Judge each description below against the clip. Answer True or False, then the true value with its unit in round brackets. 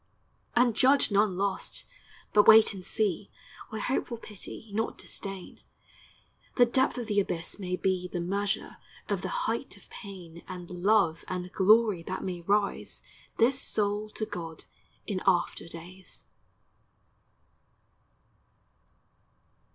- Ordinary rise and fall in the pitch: True (3.2 semitones)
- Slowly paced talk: True (125 wpm)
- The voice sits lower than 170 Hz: False (200 Hz)